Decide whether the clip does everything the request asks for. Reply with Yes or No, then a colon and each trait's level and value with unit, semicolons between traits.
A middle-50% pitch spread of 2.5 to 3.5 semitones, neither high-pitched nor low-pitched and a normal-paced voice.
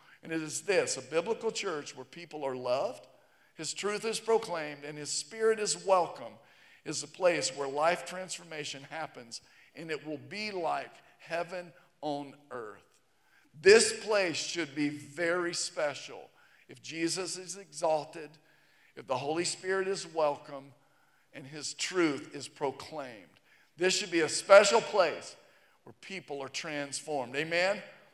No: average, 4.2 semitones; medium, 165 Hz; average, 145 wpm